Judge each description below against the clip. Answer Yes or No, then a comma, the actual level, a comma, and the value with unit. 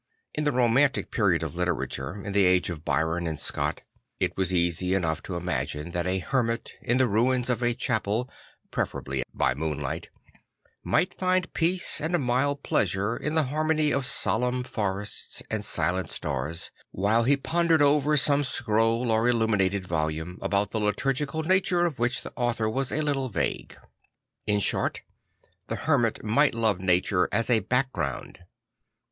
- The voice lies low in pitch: Yes, low, 115 Hz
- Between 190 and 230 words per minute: No, average, 165 wpm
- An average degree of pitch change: No, wide, 6.9 semitones